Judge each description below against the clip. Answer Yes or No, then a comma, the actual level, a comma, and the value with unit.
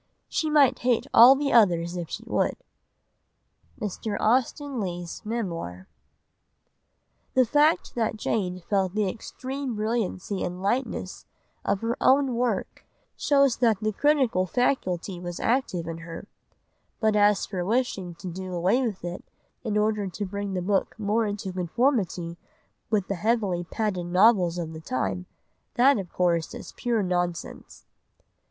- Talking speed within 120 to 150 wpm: Yes, average, 145 wpm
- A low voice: No, high, 205 Hz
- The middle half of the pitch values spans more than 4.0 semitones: Yes, average, 4.9 semitones